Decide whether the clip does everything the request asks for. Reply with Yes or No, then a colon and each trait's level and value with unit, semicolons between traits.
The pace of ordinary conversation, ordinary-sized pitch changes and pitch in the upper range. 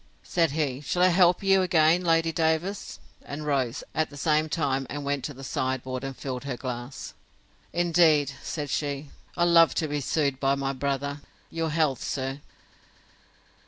No: average, 160 wpm; average, 3.3 semitones; medium, 145 Hz